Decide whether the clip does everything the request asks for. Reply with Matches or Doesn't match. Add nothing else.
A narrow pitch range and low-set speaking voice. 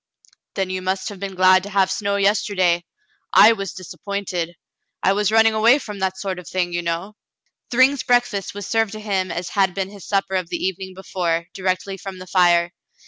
Doesn't match